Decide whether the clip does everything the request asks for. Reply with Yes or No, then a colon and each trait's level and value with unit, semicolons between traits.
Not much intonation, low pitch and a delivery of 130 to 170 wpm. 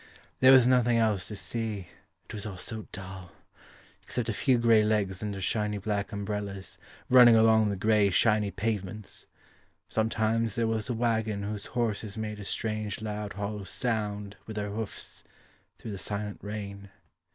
Yes: narrow, 1.7 semitones; low, 105 Hz; average, 160 wpm